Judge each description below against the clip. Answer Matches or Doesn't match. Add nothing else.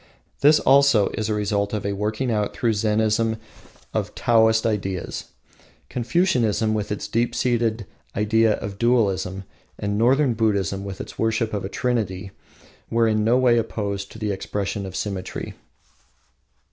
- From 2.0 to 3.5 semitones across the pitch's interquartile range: Matches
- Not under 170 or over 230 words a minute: Doesn't match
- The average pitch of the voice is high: Doesn't match